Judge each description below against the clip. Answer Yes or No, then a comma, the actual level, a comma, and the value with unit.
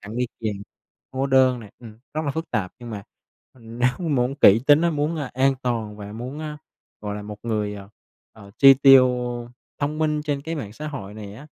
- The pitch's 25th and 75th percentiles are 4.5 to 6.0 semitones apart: Yes, average, 5.2 semitones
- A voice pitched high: No, low, 125 Hz